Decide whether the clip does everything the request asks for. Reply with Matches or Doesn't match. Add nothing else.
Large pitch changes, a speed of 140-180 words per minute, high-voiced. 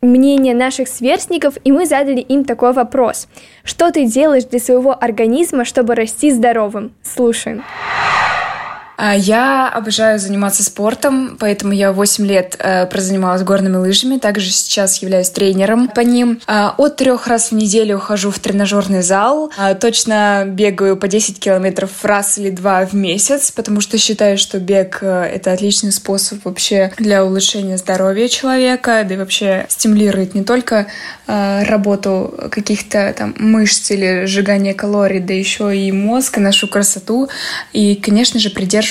Doesn't match